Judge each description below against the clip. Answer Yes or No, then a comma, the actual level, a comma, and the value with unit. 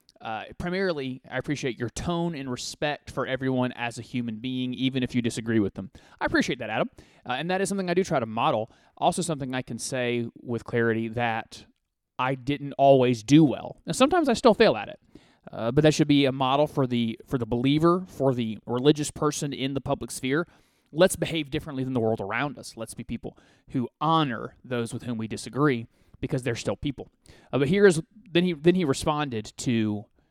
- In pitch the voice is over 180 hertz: No, low, 130 Hz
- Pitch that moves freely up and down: No, average, 4.4 semitones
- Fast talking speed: Yes, fast, 210 wpm